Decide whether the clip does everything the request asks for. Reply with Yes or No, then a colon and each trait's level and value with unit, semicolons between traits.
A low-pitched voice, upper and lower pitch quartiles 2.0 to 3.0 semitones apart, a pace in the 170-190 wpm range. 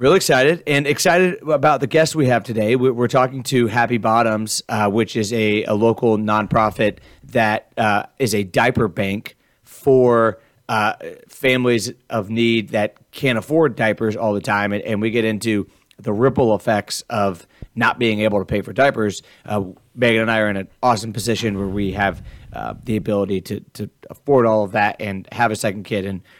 Yes: low, 110 Hz; narrow, 2.6 semitones; average, 185 wpm